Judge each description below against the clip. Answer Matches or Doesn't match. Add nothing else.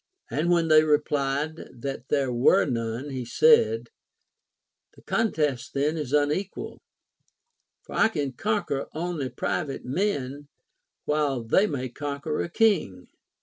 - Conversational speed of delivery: Doesn't match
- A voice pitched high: Doesn't match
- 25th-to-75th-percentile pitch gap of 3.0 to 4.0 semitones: Matches